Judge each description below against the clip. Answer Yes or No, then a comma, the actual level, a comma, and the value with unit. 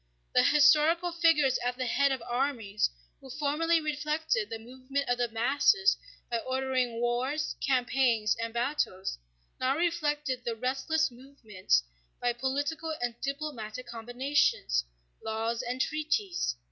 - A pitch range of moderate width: Yes, average, 3.9 semitones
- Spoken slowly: Yes, slow, 125 wpm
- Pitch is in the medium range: No, very high, 260 Hz